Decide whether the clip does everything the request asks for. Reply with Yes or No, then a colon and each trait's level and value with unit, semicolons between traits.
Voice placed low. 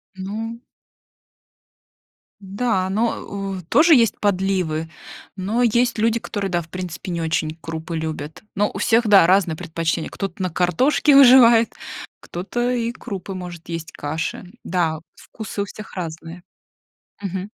No: high, 190 Hz